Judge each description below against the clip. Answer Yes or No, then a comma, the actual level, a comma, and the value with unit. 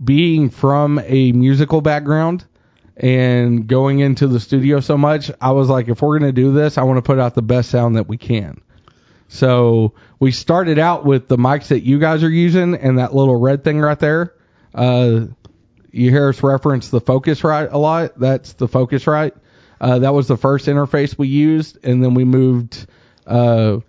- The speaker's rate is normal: Yes, average, 195 wpm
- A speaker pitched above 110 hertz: Yes, low, 135 Hz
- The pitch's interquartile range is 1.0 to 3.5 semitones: Yes, average, 3.0 semitones